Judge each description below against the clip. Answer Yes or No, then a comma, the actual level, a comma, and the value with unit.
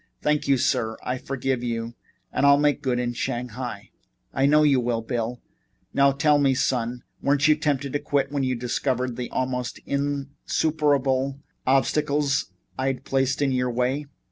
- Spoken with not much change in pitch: Yes, narrow, 2.3 semitones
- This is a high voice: No, low, 135 Hz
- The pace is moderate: Yes, average, 160 wpm